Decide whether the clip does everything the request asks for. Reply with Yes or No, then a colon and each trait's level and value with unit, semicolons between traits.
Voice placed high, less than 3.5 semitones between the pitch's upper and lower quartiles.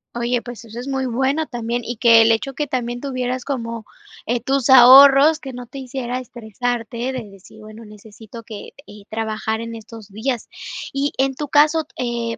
Yes: high, 240 Hz; average, 2.8 semitones